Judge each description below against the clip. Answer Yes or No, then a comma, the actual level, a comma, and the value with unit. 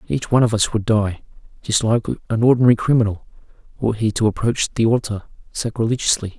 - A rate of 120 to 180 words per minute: Yes, average, 170 wpm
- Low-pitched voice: Yes, low, 110 Hz